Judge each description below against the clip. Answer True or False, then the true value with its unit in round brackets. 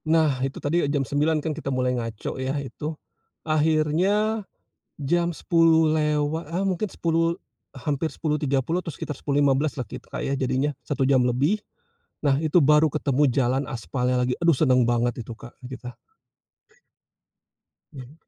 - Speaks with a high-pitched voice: False (145 Hz)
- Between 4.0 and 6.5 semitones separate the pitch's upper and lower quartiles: False (3.6 semitones)